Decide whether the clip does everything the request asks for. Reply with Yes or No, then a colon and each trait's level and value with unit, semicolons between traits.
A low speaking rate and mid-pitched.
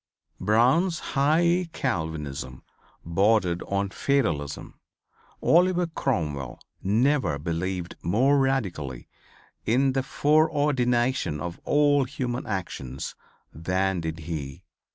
No: slow, 90 wpm; low, 110 Hz